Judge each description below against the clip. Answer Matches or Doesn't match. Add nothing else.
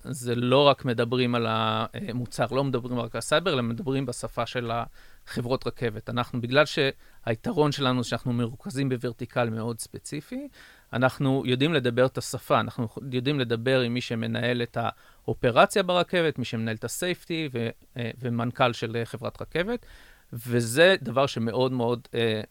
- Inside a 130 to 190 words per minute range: Matches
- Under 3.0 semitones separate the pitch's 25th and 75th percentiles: Matches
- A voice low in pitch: Matches